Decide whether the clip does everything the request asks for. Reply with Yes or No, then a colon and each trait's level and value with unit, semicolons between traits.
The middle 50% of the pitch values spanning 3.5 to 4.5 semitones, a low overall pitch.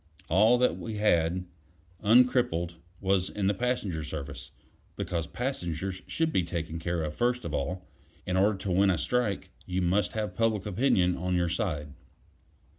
Yes: average, 4.1 semitones; very low, 95 Hz